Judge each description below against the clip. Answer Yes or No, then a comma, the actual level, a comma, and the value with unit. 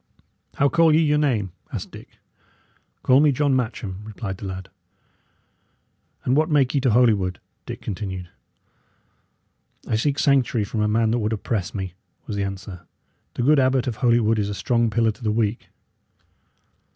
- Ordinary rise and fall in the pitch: Yes, average, 4.4 semitones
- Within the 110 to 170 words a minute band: Yes, average, 165 wpm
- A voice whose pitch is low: Yes, low, 115 Hz